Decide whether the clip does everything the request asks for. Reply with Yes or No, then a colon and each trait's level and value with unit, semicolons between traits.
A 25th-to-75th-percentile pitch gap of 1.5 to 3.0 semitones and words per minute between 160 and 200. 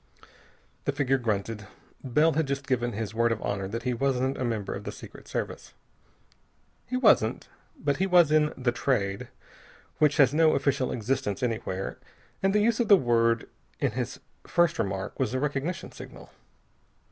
No: average, 4.9 semitones; average, 170 wpm